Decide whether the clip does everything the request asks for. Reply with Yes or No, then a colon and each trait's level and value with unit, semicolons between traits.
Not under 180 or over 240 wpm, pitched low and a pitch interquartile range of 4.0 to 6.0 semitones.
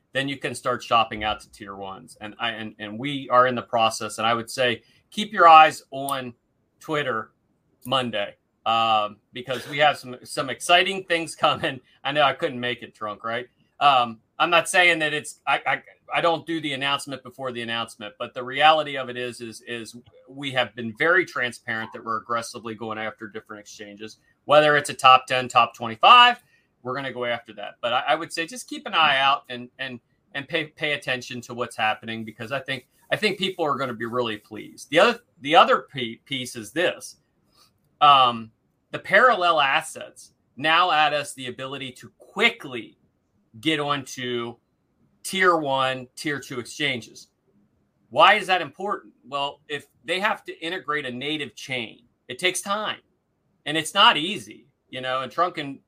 Yes: average, 185 wpm; low, 130 Hz; average, 4.5 semitones